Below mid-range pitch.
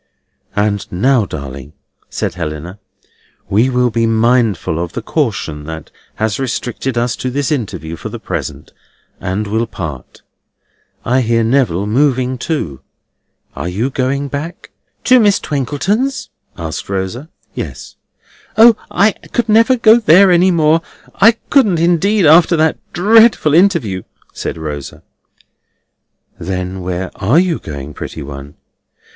Yes: low, 125 Hz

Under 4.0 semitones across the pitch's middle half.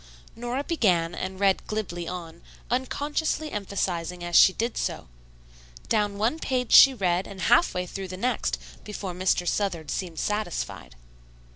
No: average, 5.2 semitones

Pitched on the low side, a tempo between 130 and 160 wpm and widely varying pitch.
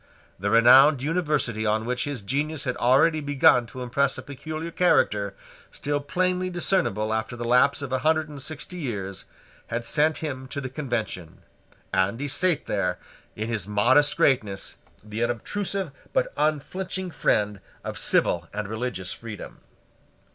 Yes: low, 130 Hz; average, 150 wpm; wide, 5.8 semitones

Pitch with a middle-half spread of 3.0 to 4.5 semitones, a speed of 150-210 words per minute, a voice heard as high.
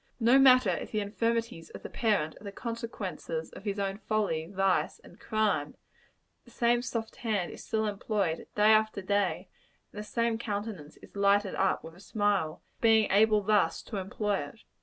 No: narrow, 2.5 semitones; average, 180 wpm; high, 210 Hz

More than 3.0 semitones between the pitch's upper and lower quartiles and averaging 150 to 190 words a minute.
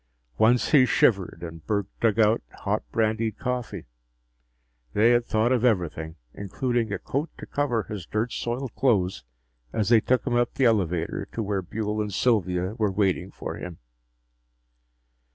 Yes: average, 3.9 semitones; average, 155 wpm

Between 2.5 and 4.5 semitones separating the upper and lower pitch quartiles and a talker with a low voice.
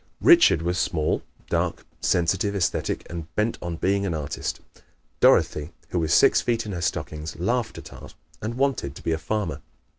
No: average, 5.0 semitones; very low, 90 Hz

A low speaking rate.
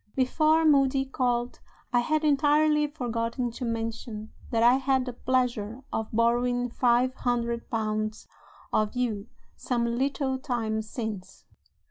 Yes: slow, 125 wpm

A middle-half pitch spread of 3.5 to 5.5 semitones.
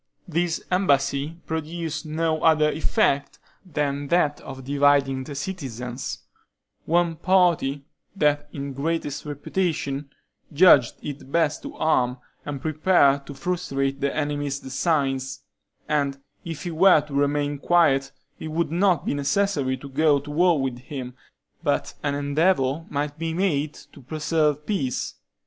No: average, 2.9 semitones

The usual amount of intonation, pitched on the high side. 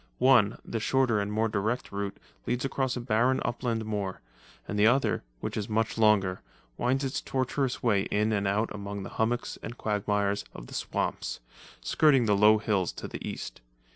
No: average, 3.2 semitones; low, 110 Hz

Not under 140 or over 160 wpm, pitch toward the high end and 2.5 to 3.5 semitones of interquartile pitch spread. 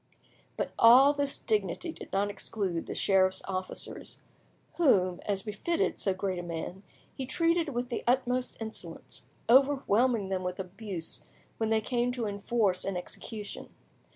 No: average, 145 wpm; high, 215 Hz; average, 4.8 semitones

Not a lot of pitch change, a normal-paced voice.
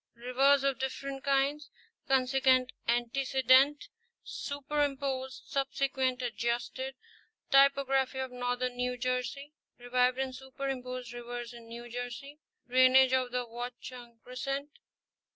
No: narrow, 1.7 semitones; slow, 100 wpm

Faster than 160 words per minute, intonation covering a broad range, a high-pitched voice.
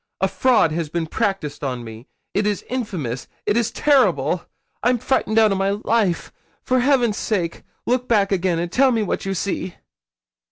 Yes: average, 175 wpm; wide, 5.8 semitones; high, 200 Hz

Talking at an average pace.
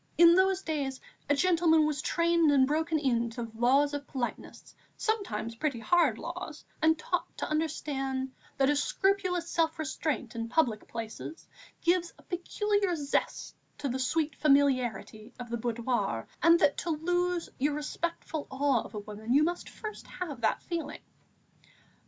Yes: average, 160 wpm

